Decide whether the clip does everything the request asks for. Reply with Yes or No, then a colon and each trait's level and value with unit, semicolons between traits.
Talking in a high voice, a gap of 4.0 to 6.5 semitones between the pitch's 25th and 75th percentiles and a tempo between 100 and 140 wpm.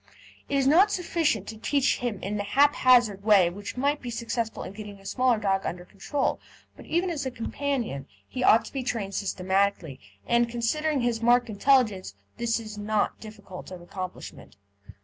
No: high, 225 Hz; average, 4.6 semitones; average, 175 wpm